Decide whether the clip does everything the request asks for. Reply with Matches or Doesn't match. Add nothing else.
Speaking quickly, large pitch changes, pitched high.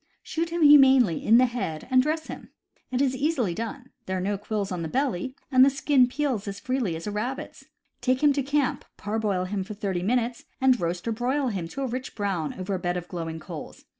Matches